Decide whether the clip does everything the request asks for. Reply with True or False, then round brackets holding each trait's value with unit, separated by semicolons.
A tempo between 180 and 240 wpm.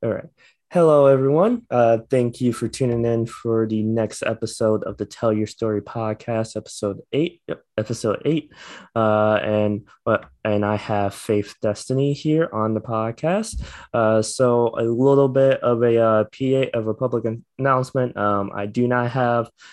False (165 wpm)